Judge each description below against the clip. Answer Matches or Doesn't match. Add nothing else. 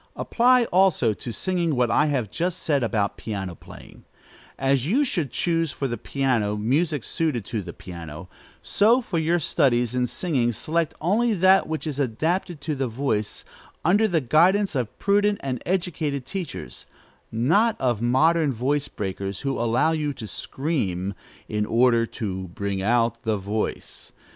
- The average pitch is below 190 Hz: Matches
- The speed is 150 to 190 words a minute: Matches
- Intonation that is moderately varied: Doesn't match